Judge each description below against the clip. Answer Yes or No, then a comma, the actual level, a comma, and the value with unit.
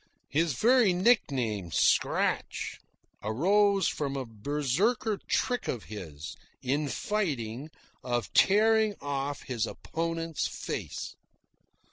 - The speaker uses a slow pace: Yes, slow, 95 wpm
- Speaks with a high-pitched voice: No, medium, 150 Hz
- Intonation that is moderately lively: No, wide, 8.5 semitones